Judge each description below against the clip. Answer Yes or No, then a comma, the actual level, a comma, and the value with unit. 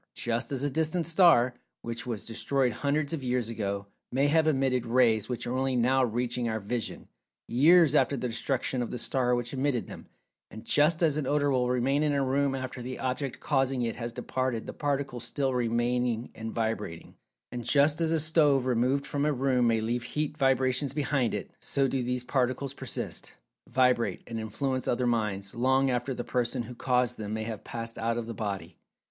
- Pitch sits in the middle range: No, low, 125 Hz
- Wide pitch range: No, average, 2.8 semitones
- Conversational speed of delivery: Yes, average, 190 wpm